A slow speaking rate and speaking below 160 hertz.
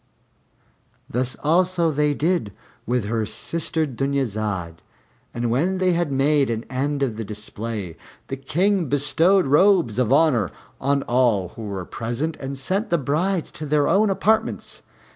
No: average, 145 wpm; medium, 140 Hz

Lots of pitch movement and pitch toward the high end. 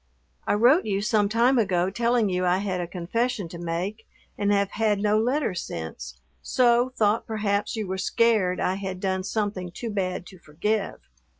No: average, 3.3 semitones; high, 200 Hz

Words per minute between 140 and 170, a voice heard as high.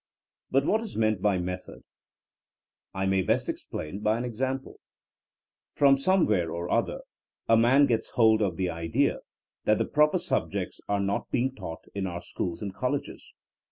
No: average, 165 wpm; low, 105 Hz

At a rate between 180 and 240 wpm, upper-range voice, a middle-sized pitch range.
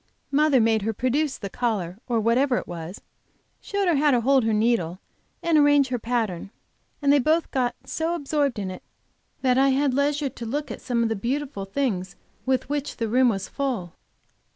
Yes: average, 195 wpm; very high, 250 Hz; average, 4.4 semitones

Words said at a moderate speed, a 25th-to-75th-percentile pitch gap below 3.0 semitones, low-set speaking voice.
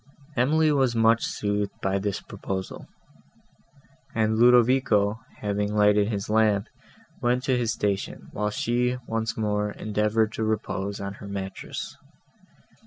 No: slow, 125 wpm; narrow, 2.4 semitones; low, 105 Hz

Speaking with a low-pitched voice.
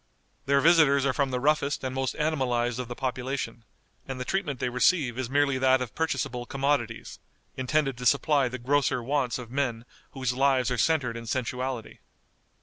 Yes: low, 130 Hz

